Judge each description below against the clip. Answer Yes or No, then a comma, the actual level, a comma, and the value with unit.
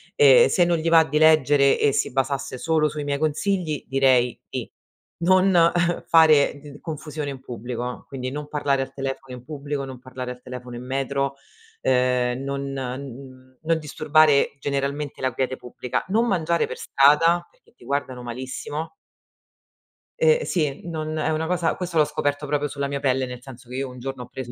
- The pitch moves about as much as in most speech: Yes, average, 3.2 semitones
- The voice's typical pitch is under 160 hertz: Yes, medium, 140 Hz